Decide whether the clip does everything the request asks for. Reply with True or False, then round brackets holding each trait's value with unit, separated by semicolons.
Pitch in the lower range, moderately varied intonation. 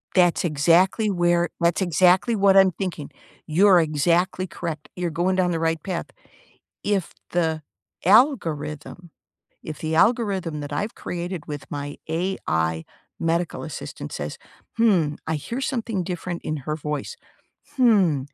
False (175 Hz; 3.4 semitones)